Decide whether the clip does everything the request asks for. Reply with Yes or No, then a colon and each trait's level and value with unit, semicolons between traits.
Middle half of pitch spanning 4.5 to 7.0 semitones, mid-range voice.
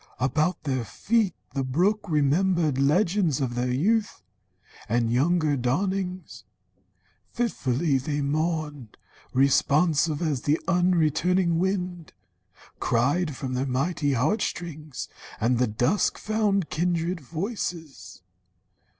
Yes: average, 5.2 semitones; medium, 155 Hz